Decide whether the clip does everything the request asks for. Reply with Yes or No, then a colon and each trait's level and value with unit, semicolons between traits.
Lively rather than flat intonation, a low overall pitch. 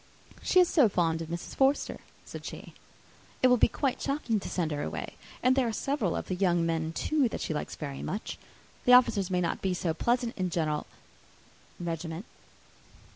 No: wide, 7.1 semitones; medium, 185 Hz